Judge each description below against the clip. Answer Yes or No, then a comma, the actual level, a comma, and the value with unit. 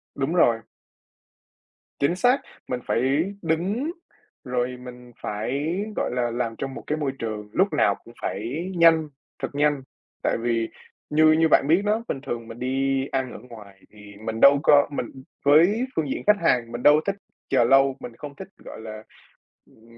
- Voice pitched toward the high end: No, low, 135 Hz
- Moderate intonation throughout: Yes, average, 5.0 semitones